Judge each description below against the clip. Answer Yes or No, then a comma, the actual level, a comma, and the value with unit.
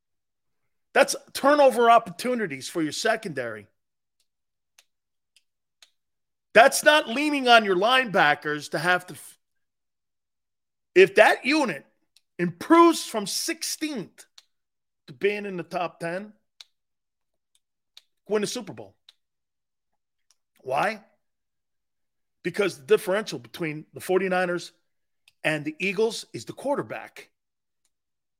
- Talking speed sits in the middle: No, slow, 95 wpm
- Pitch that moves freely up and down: Yes, wide, 6.4 semitones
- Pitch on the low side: No, high, 190 Hz